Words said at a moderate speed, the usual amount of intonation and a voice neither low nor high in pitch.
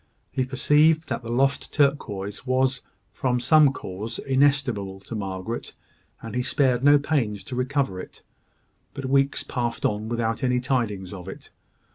No: average, 150 wpm; average, 4.3 semitones; low, 125 Hz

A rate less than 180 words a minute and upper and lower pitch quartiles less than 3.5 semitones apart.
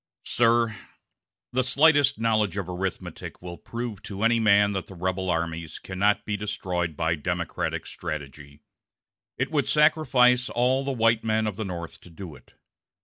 No: average, 155 wpm; average, 5.1 semitones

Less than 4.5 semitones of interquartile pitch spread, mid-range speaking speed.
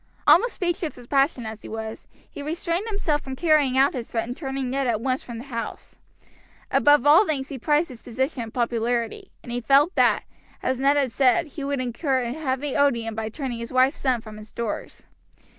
No: average, 3.6 semitones; fast, 210 wpm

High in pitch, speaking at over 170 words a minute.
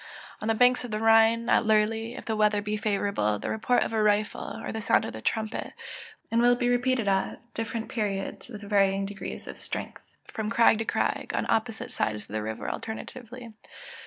Yes: high, 220 Hz; average, 200 wpm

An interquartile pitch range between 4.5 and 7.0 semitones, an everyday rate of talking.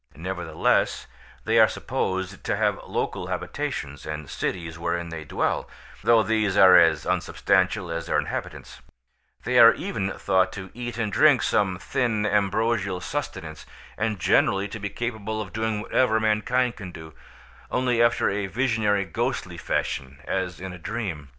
No: average, 4.1 semitones; average, 150 wpm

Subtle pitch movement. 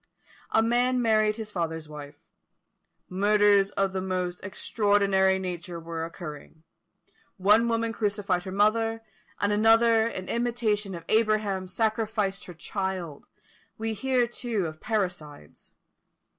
No: average, 3.5 semitones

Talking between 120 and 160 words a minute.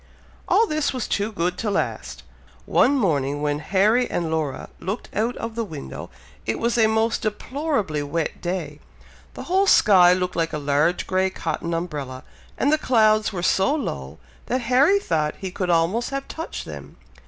No: average, 175 wpm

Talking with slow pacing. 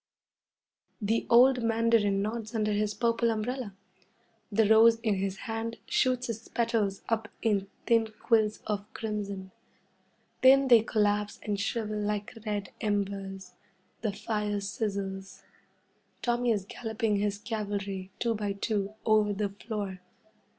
Yes: slow, 130 wpm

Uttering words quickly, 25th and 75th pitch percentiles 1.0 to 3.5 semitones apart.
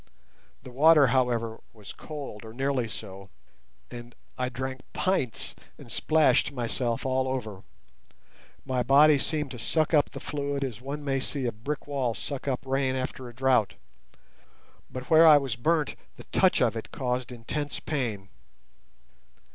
No: average, 155 wpm; average, 3.0 semitones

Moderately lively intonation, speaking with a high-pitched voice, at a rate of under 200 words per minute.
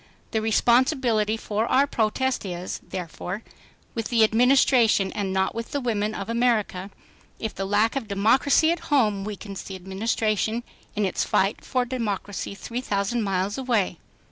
Yes: average, 3.4 semitones; high, 220 Hz; average, 150 wpm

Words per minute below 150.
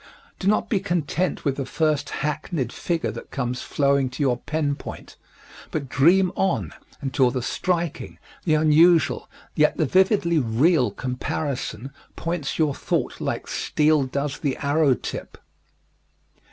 Yes: average, 140 wpm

